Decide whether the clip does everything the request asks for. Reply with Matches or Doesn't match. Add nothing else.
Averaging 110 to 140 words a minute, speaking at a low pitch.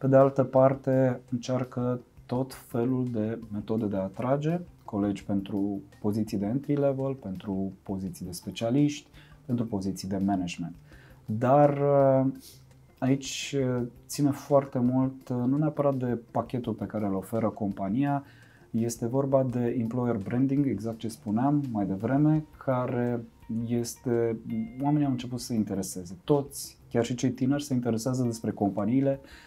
Matches